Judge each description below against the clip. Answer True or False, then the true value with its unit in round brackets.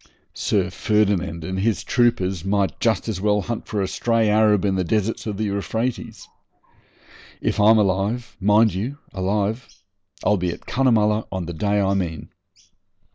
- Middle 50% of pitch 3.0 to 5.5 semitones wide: False (2.5 semitones)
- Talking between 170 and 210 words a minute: False (160 wpm)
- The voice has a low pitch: True (105 Hz)